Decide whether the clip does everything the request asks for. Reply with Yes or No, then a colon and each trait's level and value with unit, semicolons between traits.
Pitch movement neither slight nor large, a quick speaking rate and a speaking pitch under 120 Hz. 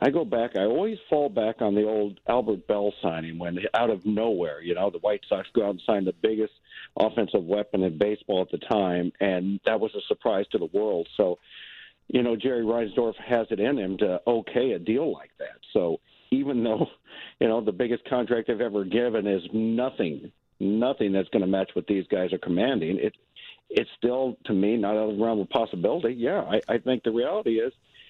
Yes: average, 3.8 semitones; fast, 215 wpm; low, 110 Hz